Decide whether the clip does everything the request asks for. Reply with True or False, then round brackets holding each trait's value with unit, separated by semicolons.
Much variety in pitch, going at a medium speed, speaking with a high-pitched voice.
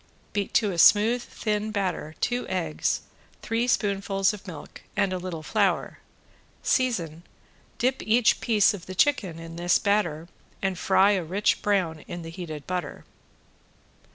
False (3.7 semitones; 150 wpm; 195 Hz)